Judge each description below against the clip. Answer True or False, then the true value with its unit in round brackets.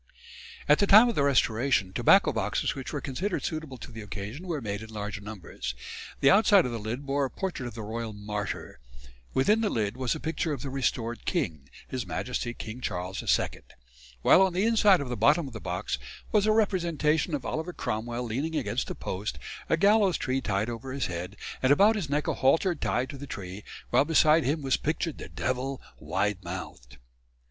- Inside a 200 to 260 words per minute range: True (205 wpm)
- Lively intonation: True (6.9 semitones)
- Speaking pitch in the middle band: False (130 Hz)